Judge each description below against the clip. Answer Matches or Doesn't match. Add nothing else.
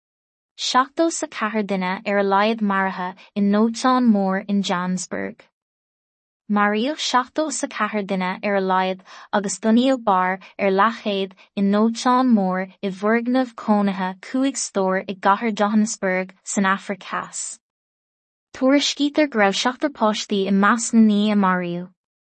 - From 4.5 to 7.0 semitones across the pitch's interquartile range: Doesn't match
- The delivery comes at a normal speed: Doesn't match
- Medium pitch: Doesn't match